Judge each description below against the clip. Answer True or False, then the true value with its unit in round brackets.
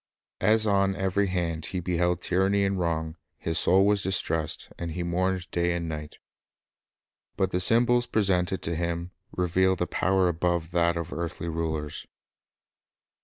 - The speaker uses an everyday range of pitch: False (2.1 semitones)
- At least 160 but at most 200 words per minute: False (150 wpm)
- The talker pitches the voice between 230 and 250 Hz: False (90 Hz)